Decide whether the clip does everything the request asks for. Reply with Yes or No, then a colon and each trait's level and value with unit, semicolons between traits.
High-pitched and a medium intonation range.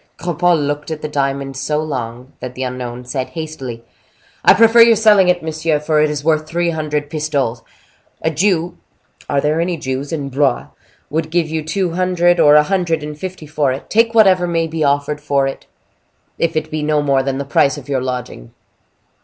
No: medium, 150 Hz; average, 3.2 semitones